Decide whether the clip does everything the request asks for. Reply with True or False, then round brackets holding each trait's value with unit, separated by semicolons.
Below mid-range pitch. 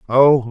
True (130 Hz)